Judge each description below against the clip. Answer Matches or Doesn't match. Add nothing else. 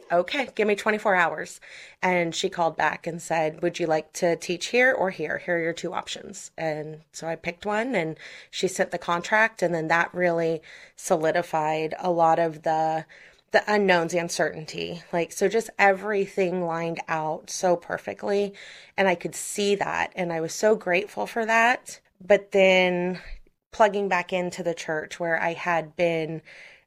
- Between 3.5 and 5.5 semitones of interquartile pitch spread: Doesn't match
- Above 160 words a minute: Matches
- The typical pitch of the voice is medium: Matches